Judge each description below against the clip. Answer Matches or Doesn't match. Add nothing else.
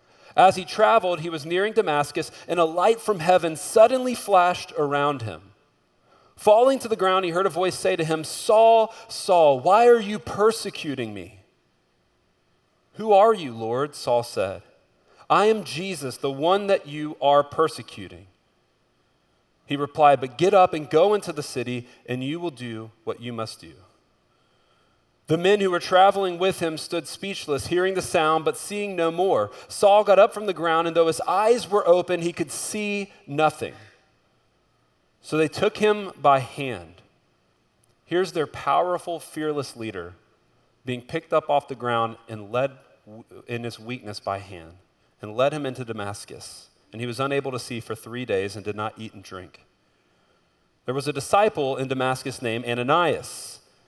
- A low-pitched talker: Doesn't match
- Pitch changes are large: Matches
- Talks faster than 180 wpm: Doesn't match